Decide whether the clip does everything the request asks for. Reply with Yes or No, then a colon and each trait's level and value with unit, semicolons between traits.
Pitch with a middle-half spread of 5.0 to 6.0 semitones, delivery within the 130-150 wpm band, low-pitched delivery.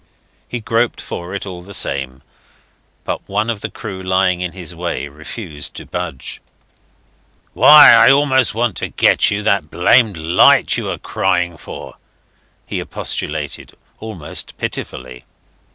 Yes: wide, 5.4 semitones; average, 140 wpm; very low, 95 Hz